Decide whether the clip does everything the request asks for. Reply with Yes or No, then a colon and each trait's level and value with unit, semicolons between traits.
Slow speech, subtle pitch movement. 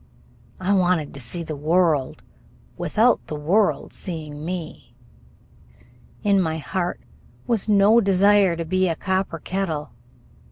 No: slow, 125 wpm; average, 3.8 semitones